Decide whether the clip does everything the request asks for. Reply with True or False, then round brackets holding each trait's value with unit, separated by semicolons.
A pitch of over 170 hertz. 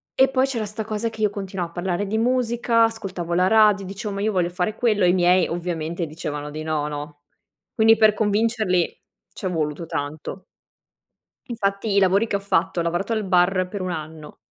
True (190 Hz)